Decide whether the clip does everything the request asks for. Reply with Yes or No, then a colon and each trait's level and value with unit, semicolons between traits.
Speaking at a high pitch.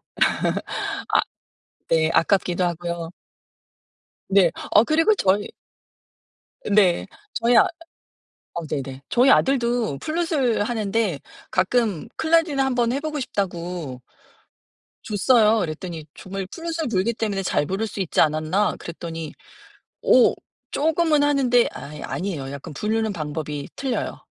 Yes: high, 200 Hz